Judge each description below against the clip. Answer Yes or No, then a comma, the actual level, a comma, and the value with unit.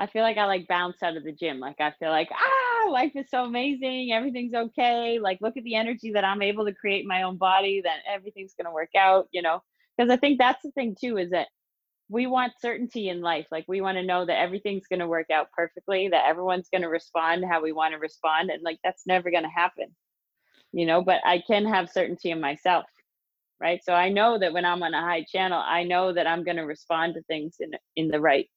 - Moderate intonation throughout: Yes, average, 4.8 semitones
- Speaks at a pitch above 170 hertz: Yes, medium, 185 Hz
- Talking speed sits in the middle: No, fast, 240 wpm